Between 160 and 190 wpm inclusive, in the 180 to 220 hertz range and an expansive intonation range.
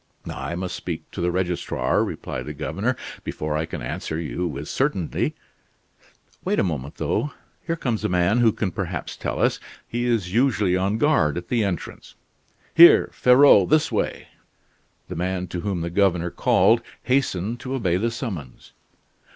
No: average, 165 wpm; very low, 95 Hz; wide, 5.7 semitones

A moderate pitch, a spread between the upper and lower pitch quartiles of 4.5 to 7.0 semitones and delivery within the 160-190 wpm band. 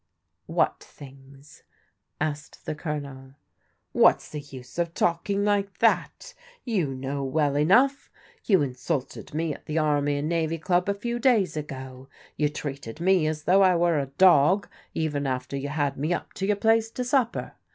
Yes: medium, 155 Hz; average, 5.2 semitones; average, 170 wpm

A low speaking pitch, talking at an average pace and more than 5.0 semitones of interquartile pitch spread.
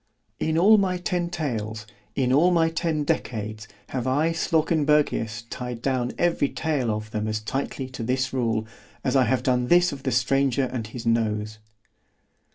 Yes: low, 130 Hz; average, 165 wpm; wide, 5.6 semitones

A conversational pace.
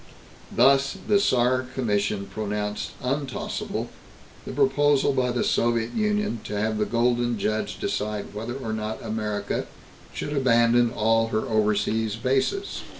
No: slow, 130 wpm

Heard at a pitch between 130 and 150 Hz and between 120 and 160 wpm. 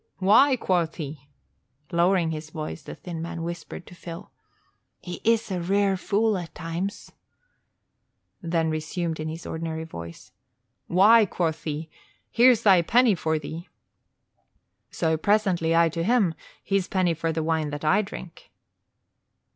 No: medium, 170 Hz; average, 140 wpm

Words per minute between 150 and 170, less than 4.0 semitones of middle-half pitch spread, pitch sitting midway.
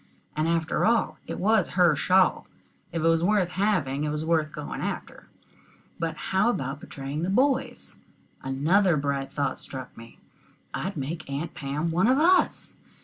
No: average, 160 wpm; average, 5.2 semitones; medium, 165 Hz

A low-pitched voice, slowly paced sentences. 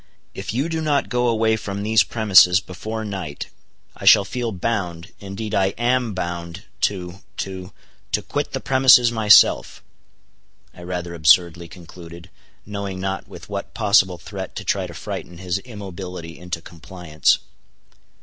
Yes: very low, 95 Hz; slow, 130 wpm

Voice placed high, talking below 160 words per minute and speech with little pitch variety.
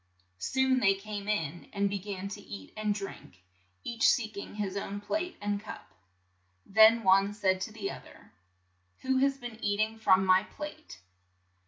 No: high, 205 Hz; average, 175 wpm; narrow, 2.2 semitones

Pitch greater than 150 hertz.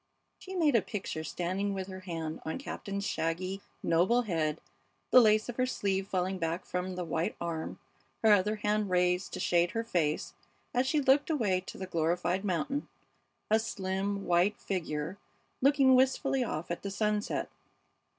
Yes: high, 190 Hz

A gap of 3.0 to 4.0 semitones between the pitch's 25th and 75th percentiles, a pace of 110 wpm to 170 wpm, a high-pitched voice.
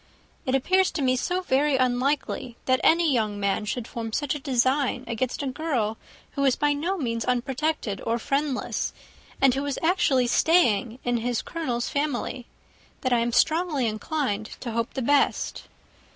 Yes: average, 3.7 semitones; average, 165 wpm; very high, 260 Hz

